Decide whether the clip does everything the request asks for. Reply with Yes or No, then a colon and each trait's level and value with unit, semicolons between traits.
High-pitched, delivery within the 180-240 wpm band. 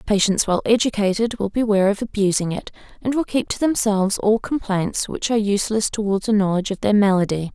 Yes: high, 210 Hz; average, 190 wpm